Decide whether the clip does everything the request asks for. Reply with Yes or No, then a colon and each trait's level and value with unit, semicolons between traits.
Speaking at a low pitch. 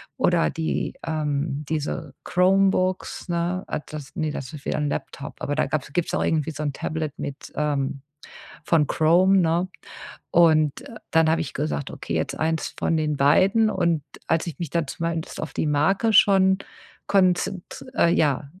No: medium, 160 Hz